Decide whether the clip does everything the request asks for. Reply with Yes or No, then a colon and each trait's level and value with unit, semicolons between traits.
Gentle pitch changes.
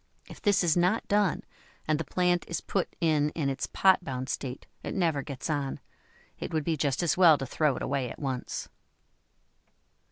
No: average, 4.3 semitones